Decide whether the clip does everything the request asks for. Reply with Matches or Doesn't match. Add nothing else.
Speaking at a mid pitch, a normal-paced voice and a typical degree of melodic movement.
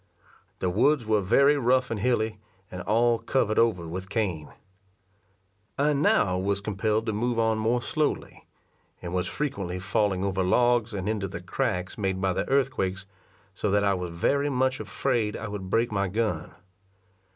Doesn't match